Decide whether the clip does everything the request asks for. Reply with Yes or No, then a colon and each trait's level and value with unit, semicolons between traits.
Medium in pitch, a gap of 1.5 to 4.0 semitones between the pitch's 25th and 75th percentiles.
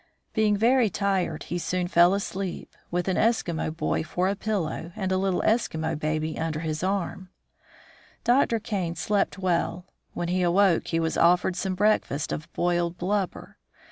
Yes: medium, 180 Hz; average, 2.9 semitones